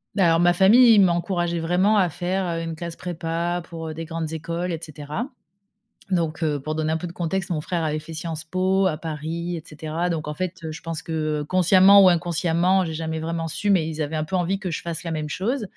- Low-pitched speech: No, medium, 170 Hz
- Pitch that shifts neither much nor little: No, narrow, 2.3 semitones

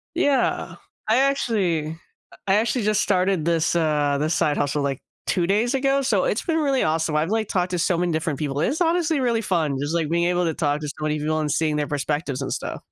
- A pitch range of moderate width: No, wide, 6.5 semitones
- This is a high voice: No, medium, 170 Hz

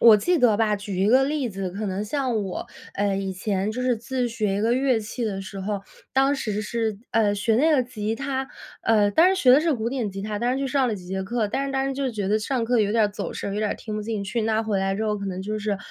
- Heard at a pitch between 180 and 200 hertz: No, high, 220 Hz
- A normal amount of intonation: Yes, average, 3.7 semitones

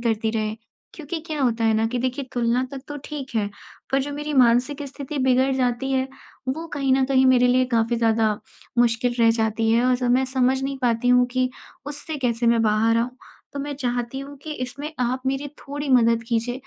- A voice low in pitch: No, very high, 250 Hz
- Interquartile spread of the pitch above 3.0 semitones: No, average, 2.7 semitones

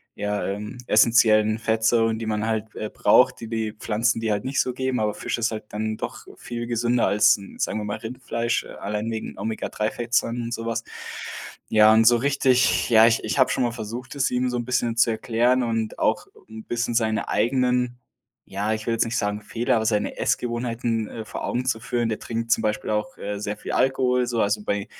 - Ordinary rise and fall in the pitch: No, narrow, 2.0 semitones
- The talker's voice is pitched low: Yes, low, 115 Hz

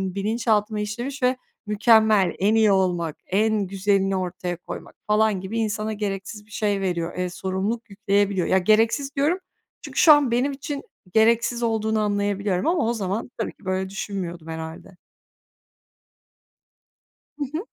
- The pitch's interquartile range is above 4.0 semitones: No, average, 2.9 semitones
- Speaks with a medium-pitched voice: No, high, 210 Hz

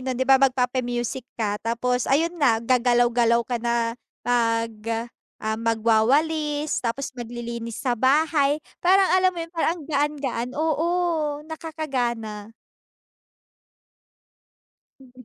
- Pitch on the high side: Yes, very high, 250 Hz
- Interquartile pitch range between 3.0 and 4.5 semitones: Yes, average, 4.0 semitones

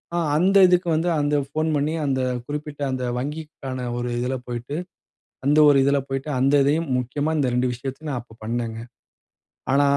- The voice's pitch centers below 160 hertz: Yes, medium, 140 Hz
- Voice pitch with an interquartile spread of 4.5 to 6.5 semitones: No, average, 3.0 semitones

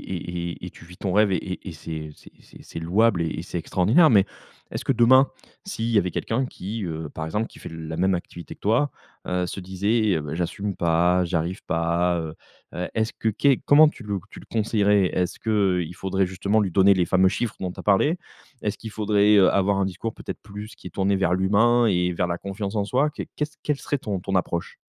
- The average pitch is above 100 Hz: No, very low, 95 Hz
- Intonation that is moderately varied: Yes, average, 3.6 semitones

